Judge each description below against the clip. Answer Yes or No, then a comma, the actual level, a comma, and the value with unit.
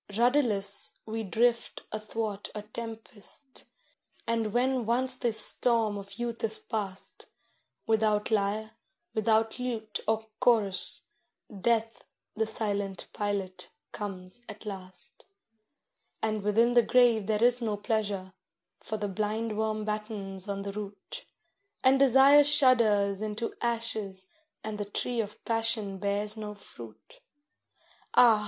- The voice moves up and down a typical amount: No, narrow, 2.2 semitones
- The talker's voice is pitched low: No, high, 215 Hz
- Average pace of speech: No, slow, 120 wpm